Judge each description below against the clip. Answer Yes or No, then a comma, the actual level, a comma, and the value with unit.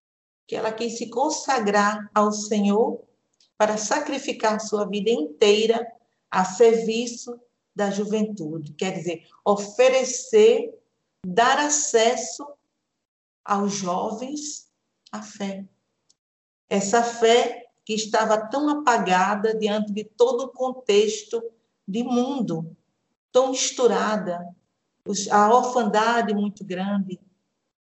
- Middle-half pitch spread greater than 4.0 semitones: No, average, 3.2 semitones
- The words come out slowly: Yes, slow, 95 wpm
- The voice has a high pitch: Yes, high, 225 Hz